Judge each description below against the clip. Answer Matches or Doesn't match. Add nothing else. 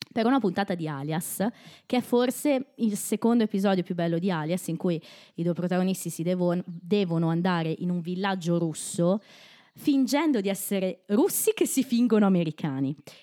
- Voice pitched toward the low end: Doesn't match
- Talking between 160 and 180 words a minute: Matches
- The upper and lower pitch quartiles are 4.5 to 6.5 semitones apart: Matches